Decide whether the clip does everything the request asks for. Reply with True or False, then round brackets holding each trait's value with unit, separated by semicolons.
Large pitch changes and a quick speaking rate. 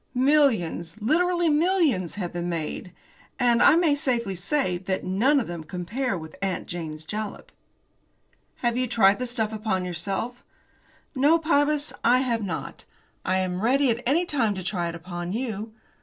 False (6.9 semitones; 165 wpm)